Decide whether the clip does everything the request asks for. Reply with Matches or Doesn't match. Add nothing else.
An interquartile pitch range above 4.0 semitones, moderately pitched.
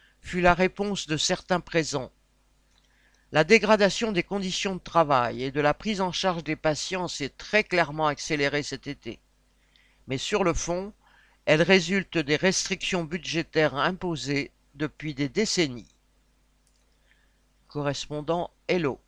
Matches